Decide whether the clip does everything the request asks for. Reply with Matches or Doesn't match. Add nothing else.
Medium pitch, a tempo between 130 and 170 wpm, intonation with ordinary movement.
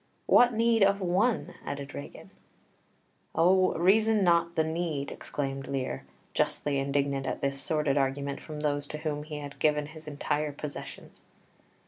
Matches